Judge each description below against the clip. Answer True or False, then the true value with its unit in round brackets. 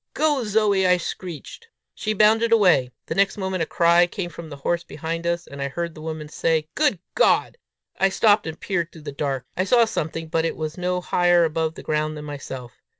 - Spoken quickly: True (210 wpm)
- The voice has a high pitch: False (170 Hz)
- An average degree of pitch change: True (3.7 semitones)